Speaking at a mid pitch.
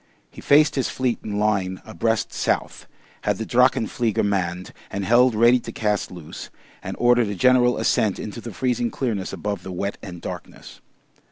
No: low, 110 Hz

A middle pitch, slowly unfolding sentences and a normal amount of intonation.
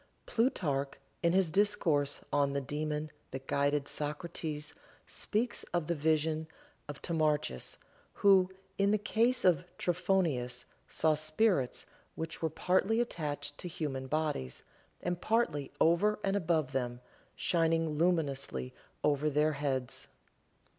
Yes: medium, 155 Hz; slow, 120 wpm; average, 3.7 semitones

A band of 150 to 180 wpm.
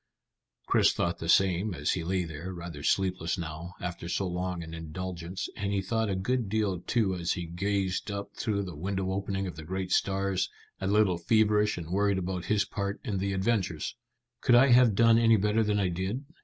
No: average, 200 wpm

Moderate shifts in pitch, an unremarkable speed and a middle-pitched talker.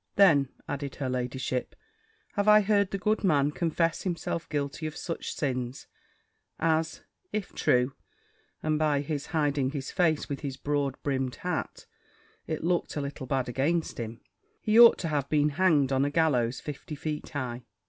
Yes: average, 3.4 semitones; average, 165 wpm; medium, 145 Hz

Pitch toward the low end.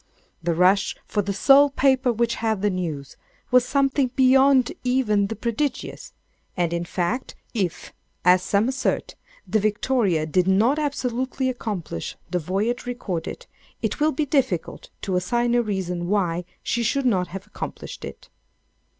No: high, 215 Hz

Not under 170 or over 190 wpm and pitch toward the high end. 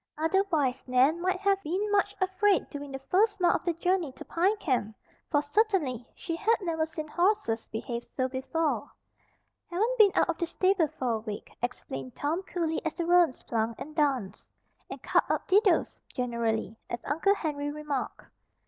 Yes: average, 175 wpm; very high, 320 Hz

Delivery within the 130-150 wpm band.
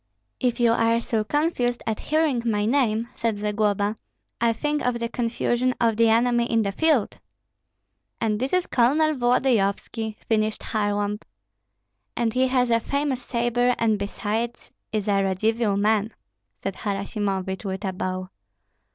Yes: average, 145 wpm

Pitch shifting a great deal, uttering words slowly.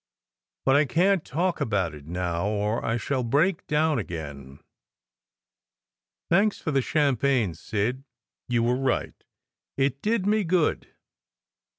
Yes: wide, 7.4 semitones; slow, 130 wpm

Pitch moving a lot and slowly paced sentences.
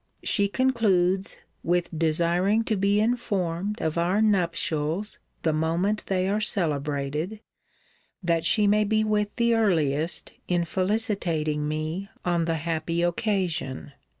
No: average, 4.3 semitones; slow, 125 wpm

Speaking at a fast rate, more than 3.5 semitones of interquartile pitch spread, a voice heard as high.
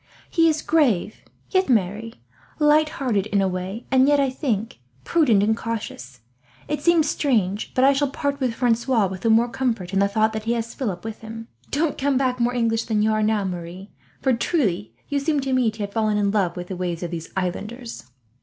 Yes: fast, 215 wpm; average, 5.0 semitones; high, 225 Hz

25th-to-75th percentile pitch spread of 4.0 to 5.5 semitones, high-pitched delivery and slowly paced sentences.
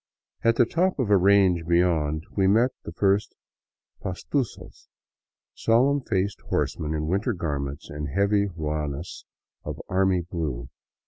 No: average, 4.8 semitones; very low, 95 Hz; slow, 130 wpm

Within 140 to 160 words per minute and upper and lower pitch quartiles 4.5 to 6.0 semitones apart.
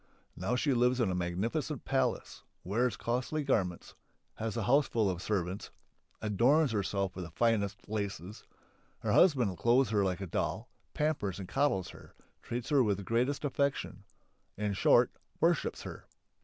Yes: average, 155 wpm; average, 5.1 semitones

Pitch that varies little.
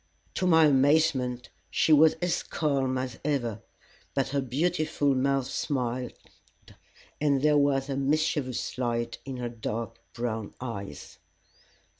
No: average, 3.2 semitones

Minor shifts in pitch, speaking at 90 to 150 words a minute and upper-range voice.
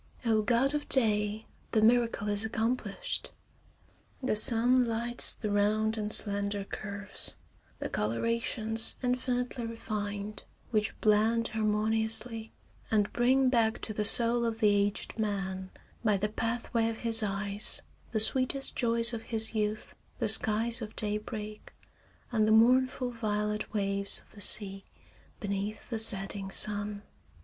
Yes: narrow, 1.9 semitones; slow, 135 wpm; high, 220 Hz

